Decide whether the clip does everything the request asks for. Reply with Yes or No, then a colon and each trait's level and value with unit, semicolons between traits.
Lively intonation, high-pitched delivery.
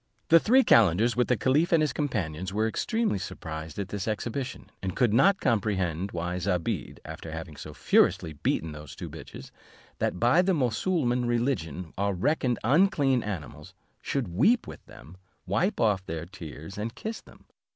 No: wide, 7.2 semitones; low, 105 Hz